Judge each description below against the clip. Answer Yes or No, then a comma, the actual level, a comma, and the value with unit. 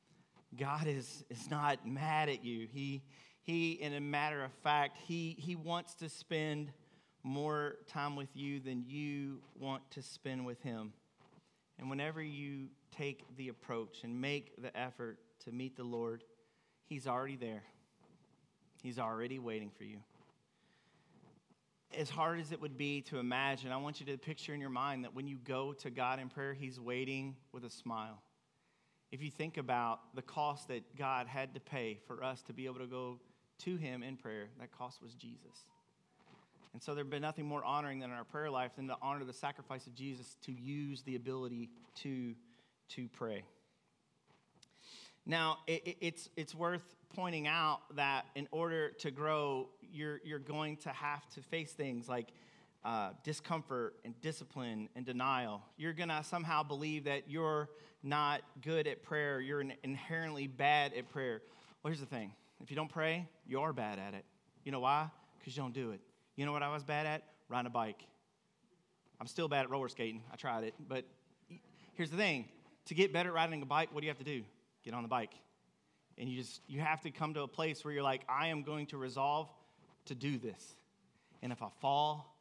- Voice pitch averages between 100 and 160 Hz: Yes, medium, 140 Hz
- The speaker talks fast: No, average, 190 wpm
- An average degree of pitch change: Yes, average, 3.3 semitones